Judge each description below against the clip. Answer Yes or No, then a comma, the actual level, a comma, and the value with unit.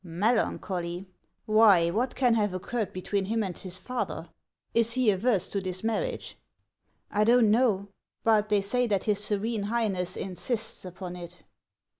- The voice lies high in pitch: Yes, high, 210 Hz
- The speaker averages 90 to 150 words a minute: No, average, 175 wpm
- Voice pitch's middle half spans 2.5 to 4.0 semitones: Yes, average, 3.5 semitones